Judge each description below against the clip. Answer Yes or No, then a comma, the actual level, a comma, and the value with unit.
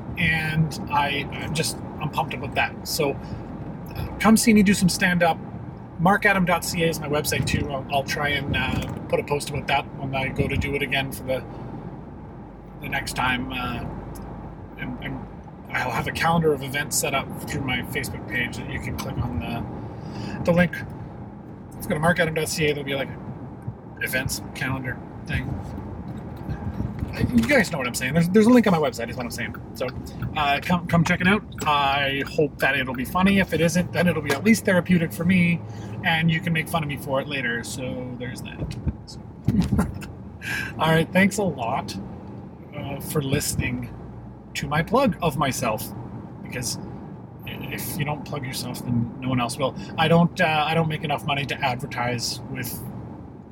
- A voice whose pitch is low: No, medium, 150 Hz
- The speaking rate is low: No, average, 185 wpm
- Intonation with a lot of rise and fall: No, average, 4.6 semitones